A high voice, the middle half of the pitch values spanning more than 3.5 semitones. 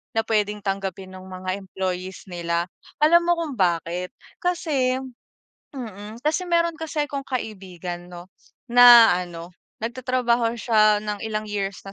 Yes: high, 210 Hz; wide, 5.4 semitones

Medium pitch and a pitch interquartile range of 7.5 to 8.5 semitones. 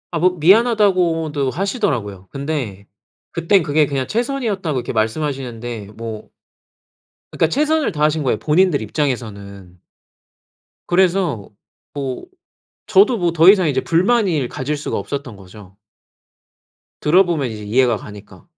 Yes: medium, 150 Hz; wide, 8.0 semitones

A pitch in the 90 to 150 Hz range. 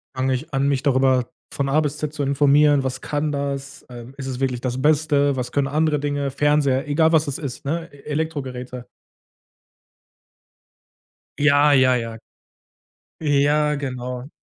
Yes: medium, 140 Hz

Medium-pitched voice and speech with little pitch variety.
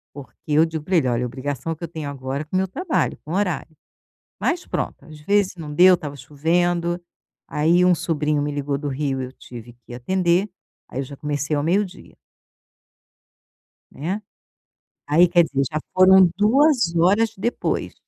No: medium, 160 Hz; average, 4.2 semitones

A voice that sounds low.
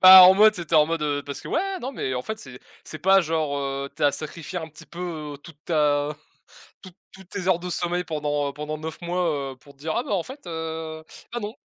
No: medium, 160 Hz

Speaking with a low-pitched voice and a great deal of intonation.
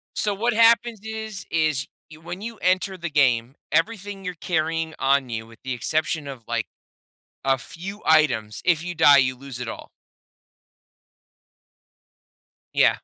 No: medium, 160 Hz; wide, 6.5 semitones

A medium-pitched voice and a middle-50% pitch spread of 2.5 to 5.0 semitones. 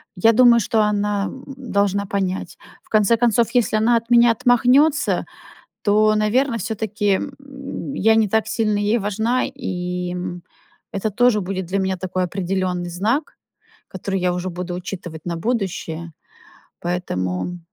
No: high, 205 Hz; average, 4.1 semitones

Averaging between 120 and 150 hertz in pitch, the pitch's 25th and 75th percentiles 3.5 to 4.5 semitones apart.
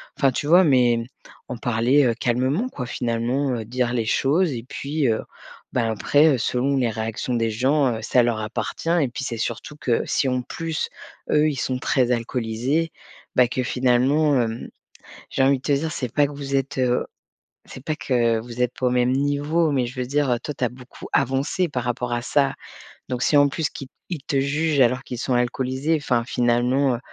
No: low, 130 Hz; average, 2.8 semitones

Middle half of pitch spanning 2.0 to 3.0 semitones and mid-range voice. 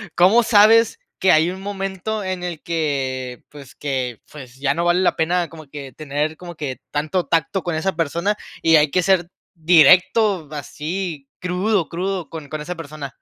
No: average, 3.9 semitones; medium, 165 Hz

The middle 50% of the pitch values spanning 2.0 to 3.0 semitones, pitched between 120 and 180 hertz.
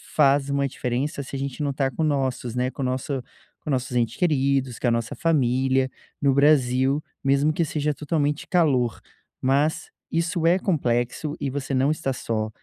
Yes: average, 2.7 semitones; low, 135 Hz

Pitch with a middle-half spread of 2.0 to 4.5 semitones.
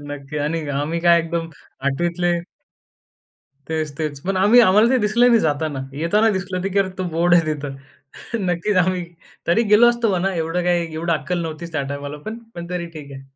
Yes: average, 3.6 semitones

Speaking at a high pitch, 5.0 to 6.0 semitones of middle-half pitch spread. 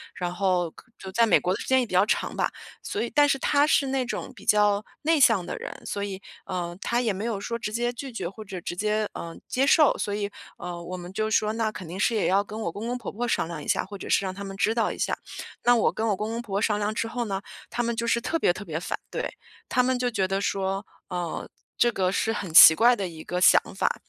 No: high, 210 Hz; average, 3.9 semitones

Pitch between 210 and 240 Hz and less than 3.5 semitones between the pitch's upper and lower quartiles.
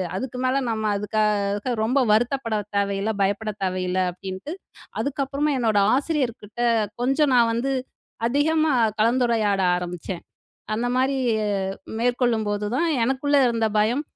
No: high, 230 Hz; average, 4.3 semitones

